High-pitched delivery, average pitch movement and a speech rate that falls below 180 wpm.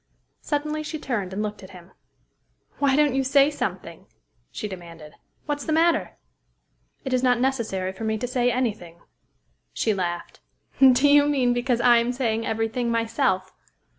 Yes: high, 245 Hz; average, 4.5 semitones; average, 165 wpm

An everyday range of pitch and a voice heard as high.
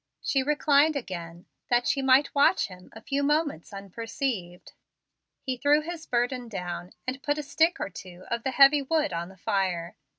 No: wide, 7.4 semitones; very high, 255 Hz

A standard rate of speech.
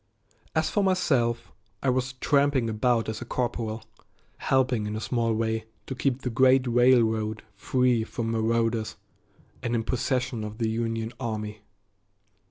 Yes: average, 145 wpm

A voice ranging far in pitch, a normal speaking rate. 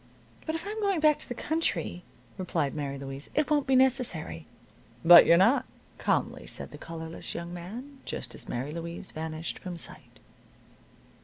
Yes: wide, 8.8 semitones; average, 165 wpm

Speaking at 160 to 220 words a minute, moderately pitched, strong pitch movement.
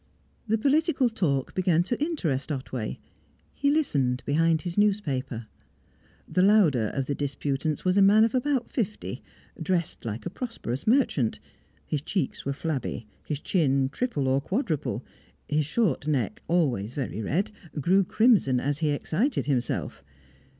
No: average, 145 wpm; medium, 160 Hz; wide, 7.7 semitones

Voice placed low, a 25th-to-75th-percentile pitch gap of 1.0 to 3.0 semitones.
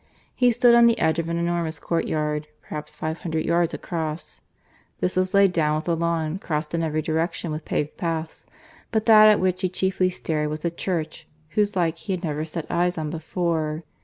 No: medium, 165 Hz; narrow, 2.6 semitones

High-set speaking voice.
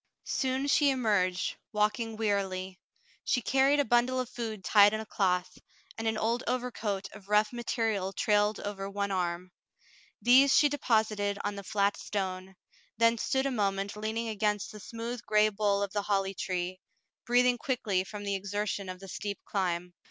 Yes: high, 210 Hz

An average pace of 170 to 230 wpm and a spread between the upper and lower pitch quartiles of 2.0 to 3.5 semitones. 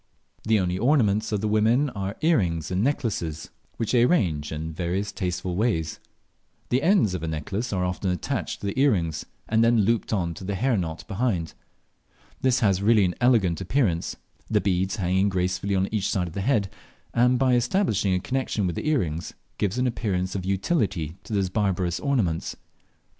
No: average, 180 wpm; average, 4.6 semitones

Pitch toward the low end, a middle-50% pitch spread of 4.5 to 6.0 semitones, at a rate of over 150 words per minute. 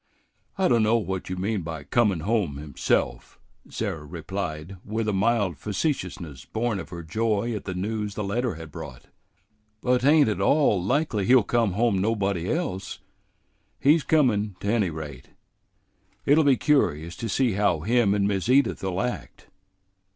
Yes: low, 105 Hz; average, 4.9 semitones; average, 160 wpm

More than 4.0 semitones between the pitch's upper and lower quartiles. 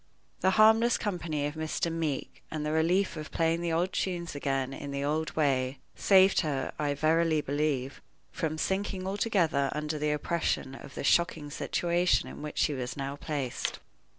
No: average, 3.3 semitones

